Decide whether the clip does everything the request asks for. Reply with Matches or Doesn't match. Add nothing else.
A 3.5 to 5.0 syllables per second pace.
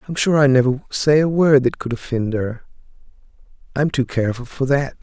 Doesn't match